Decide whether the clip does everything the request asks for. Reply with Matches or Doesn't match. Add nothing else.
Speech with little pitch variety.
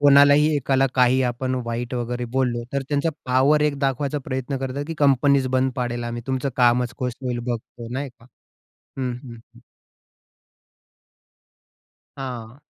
Matches